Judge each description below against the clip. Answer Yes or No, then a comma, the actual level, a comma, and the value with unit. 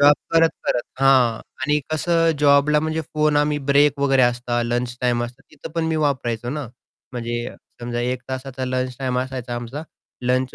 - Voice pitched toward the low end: Yes, low, 130 Hz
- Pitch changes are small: No, average, 3.3 semitones